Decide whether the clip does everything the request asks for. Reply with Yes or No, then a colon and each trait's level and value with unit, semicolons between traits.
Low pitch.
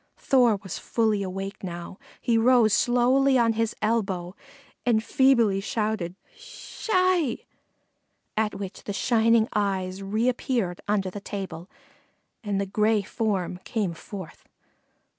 No: high, 215 Hz